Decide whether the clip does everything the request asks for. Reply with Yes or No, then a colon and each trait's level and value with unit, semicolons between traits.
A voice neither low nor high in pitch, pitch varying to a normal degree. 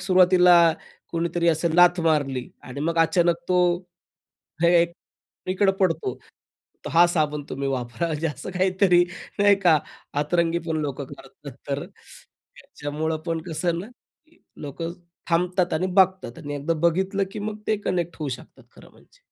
Yes: medium, 170 Hz; average, 3.0 semitones